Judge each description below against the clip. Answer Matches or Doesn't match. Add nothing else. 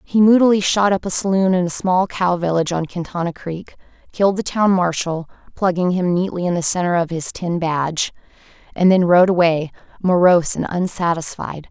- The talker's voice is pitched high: Doesn't match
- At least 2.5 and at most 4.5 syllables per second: Matches